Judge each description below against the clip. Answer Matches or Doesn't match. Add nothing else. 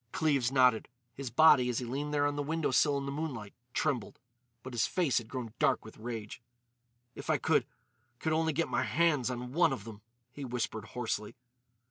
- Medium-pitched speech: Doesn't match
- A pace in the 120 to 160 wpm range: Doesn't match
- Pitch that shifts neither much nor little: Matches